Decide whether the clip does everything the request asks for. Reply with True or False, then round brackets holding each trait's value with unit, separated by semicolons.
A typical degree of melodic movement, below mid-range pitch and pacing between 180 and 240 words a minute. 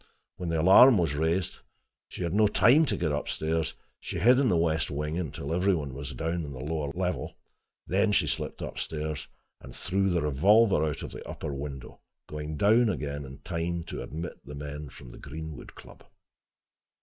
True (4.1 semitones; 80 Hz; 195 wpm)